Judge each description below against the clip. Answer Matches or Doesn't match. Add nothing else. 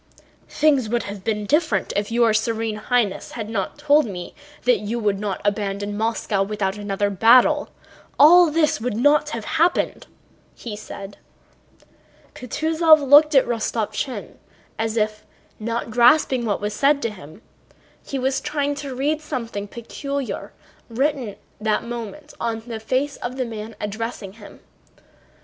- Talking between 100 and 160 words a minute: Matches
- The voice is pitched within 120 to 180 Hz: Doesn't match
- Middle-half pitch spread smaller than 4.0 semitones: Doesn't match